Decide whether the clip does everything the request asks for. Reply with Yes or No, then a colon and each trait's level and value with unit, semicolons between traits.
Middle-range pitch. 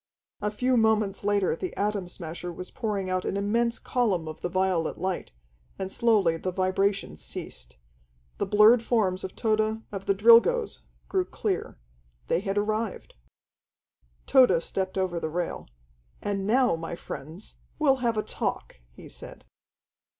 No: high, 200 Hz